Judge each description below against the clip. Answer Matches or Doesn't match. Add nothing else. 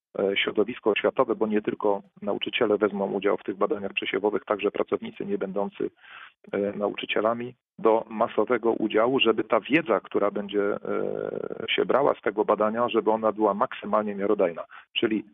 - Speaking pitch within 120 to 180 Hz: Doesn't match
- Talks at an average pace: Matches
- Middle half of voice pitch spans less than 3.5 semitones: Matches